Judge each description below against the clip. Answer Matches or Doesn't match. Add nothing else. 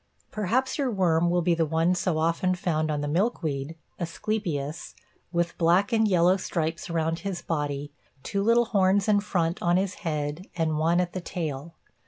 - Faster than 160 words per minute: Matches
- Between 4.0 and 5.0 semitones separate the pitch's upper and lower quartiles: Doesn't match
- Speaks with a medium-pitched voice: Matches